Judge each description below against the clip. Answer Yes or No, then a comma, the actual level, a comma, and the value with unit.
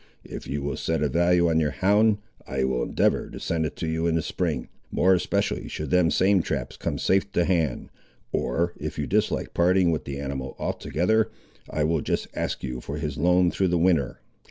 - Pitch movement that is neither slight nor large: Yes, average, 3.7 semitones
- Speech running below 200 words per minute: No, fast, 205 wpm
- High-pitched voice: No, very low, 85 Hz